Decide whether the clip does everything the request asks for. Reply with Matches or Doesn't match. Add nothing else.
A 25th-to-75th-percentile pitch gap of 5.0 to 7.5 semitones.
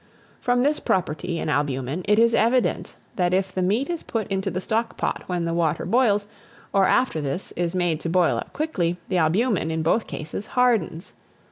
Matches